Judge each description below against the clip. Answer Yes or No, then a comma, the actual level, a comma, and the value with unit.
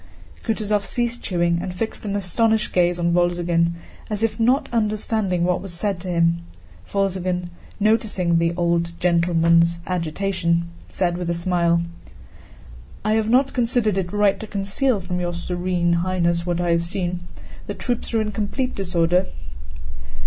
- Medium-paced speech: Yes, average, 150 wpm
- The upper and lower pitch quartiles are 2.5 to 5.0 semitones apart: Yes, average, 3.5 semitones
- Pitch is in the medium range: Yes, medium, 180 Hz